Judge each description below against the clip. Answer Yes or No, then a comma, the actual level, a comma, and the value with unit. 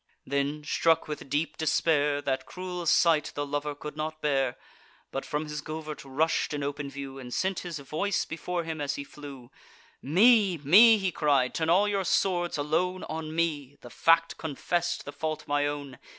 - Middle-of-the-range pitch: Yes, medium, 150 Hz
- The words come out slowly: No, average, 170 wpm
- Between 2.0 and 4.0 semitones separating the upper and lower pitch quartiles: Yes, average, 2.8 semitones